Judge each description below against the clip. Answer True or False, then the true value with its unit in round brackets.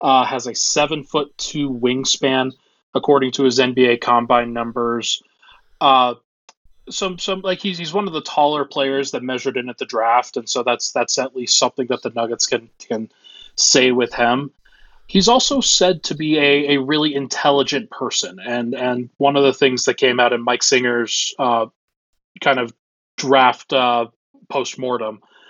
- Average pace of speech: True (175 wpm)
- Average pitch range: True (3.1 semitones)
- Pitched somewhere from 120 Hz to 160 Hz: True (135 Hz)